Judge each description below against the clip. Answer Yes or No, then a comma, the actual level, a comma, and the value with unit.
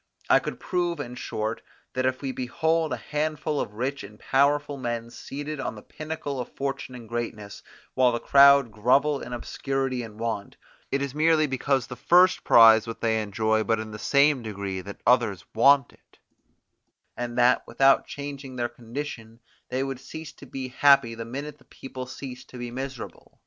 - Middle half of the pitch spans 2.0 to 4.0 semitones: Yes, average, 3.4 semitones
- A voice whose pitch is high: No, low, 130 Hz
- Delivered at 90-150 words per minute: No, average, 180 wpm